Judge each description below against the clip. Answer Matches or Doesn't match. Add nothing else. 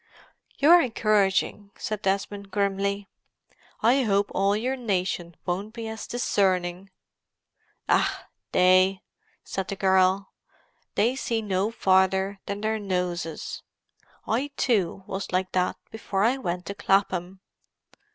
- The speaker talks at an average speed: Doesn't match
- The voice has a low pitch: Doesn't match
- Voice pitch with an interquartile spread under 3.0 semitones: Matches